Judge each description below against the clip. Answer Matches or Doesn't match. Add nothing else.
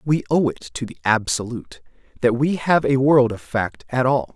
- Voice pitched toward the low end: Matches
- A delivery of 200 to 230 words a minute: Matches